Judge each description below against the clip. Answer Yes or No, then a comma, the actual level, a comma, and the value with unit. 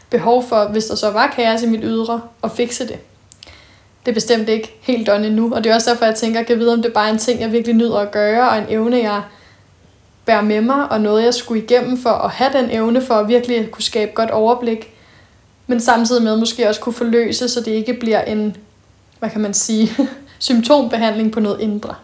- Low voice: No, high, 225 Hz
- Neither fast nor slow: No, fast, 235 wpm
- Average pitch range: No, narrow, 2.0 semitones